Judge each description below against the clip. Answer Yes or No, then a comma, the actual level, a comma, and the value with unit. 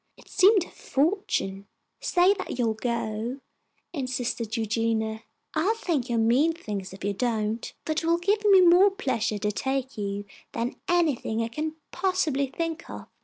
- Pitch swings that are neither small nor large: No, wide, 7.4 semitones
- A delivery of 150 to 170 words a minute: Yes, average, 165 wpm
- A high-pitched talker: Yes, very high, 255 Hz